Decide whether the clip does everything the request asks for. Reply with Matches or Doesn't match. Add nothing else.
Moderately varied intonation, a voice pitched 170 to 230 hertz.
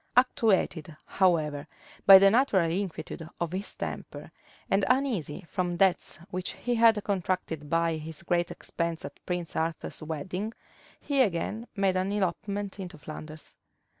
Matches